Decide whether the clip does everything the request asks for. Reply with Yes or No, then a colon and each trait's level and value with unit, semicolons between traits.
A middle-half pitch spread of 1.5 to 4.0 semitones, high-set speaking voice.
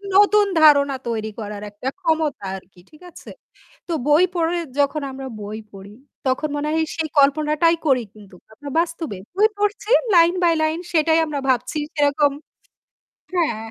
No: average, 4.5 semitones; very high, 300 Hz